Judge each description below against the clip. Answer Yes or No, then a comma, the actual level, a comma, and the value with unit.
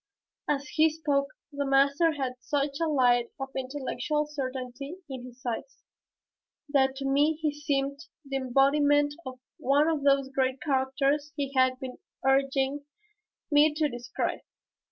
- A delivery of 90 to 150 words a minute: Yes, average, 140 wpm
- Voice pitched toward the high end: Yes, very high, 275 Hz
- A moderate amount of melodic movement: No, narrow, 1.7 semitones